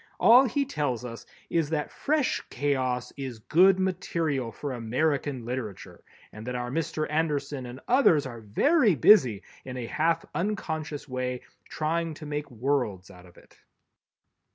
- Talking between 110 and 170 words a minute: Yes, average, 150 wpm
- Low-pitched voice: No, medium, 145 Hz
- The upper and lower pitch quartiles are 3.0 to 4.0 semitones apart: No, average, 4.9 semitones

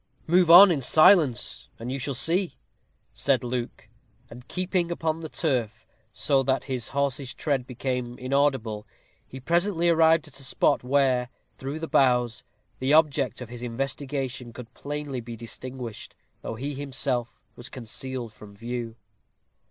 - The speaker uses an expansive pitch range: No, average, 3.3 semitones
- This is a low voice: Yes, low, 130 Hz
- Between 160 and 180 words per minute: No, average, 145 wpm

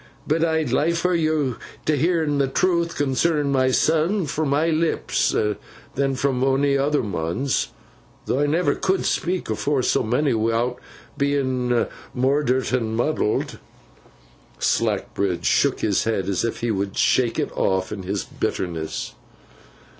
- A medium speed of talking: No, slow, 130 wpm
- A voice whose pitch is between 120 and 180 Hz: Yes, low, 135 Hz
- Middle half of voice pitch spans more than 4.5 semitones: Yes, average, 5.1 semitones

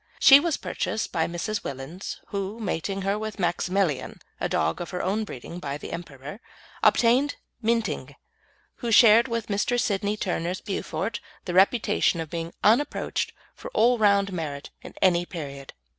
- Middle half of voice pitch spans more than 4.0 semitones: Yes, average, 4.5 semitones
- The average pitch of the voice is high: Yes, high, 195 Hz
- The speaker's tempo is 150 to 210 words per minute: Yes, average, 155 wpm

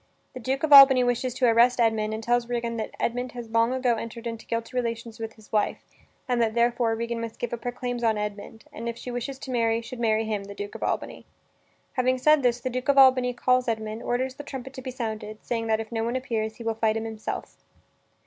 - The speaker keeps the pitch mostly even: Yes, narrow, 2.0 semitones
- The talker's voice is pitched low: No, high, 235 Hz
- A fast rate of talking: Yes, fast, 240 wpm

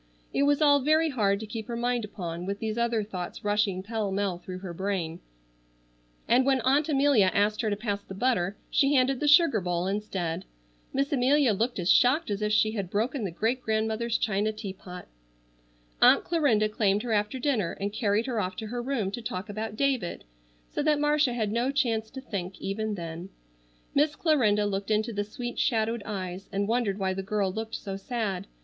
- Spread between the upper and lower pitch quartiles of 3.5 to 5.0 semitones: Yes, average, 4.0 semitones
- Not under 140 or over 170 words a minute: No, average, 195 wpm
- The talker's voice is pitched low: No, high, 215 Hz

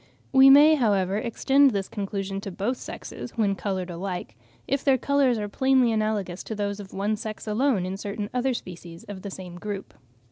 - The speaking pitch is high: Yes, high, 205 Hz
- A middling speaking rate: Yes, average, 185 wpm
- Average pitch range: Yes, average, 4.3 semitones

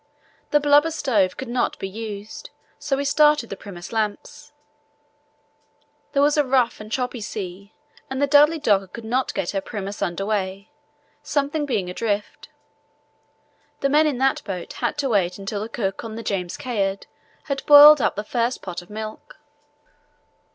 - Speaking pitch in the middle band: No, high, 225 Hz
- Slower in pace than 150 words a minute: No, average, 165 wpm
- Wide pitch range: Yes, wide, 5.9 semitones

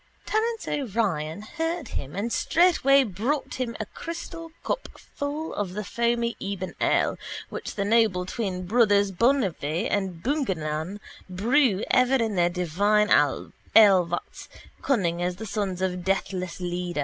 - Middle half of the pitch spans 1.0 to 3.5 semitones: No, wide, 5.5 semitones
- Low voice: No, high, 205 Hz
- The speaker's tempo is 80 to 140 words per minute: Yes, slow, 135 wpm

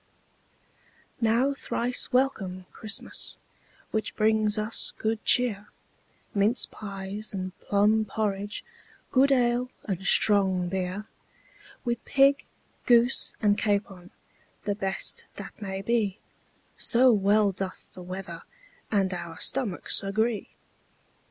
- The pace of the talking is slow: Yes, slow, 105 wpm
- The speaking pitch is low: No, high, 210 Hz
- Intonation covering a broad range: No, average, 3.3 semitones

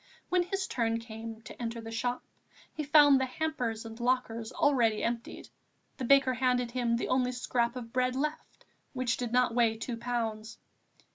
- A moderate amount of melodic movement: No, narrow, 2.0 semitones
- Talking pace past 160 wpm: Yes, average, 170 wpm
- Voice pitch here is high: Yes, high, 245 Hz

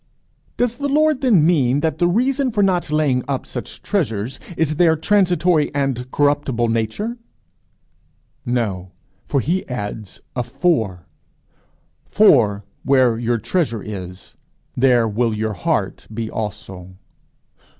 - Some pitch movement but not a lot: No, wide, 7.8 semitones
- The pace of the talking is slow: Yes, slow, 120 wpm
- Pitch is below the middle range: Yes, low, 130 Hz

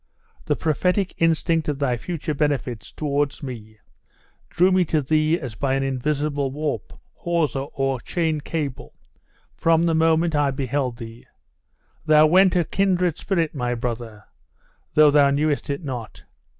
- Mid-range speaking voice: Yes, medium, 145 Hz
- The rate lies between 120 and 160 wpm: Yes, average, 145 wpm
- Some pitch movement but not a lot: Yes, average, 3.4 semitones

